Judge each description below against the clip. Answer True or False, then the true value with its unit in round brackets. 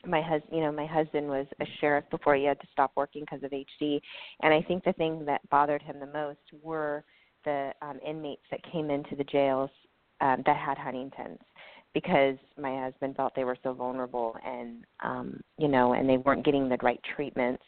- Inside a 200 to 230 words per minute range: True (205 wpm)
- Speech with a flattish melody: True (2.1 semitones)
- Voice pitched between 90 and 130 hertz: False (140 Hz)